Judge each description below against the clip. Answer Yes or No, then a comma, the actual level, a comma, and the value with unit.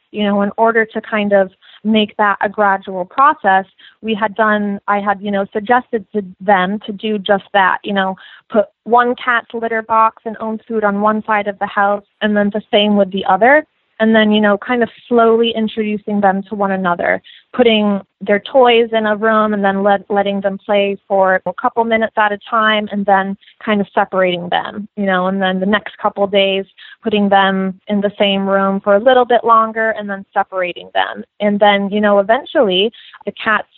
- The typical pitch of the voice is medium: No, high, 210 Hz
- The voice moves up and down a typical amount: No, narrow, 2.0 semitones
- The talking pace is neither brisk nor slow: No, fast, 210 wpm